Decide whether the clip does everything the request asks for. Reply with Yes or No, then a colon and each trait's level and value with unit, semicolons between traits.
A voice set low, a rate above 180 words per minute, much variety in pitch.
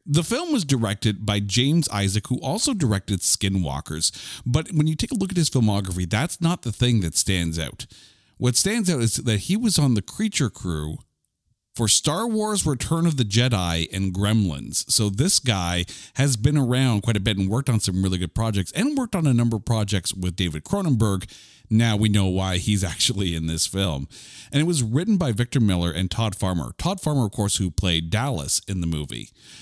Yes: low, 110 Hz; fast, 205 wpm; wide, 6.3 semitones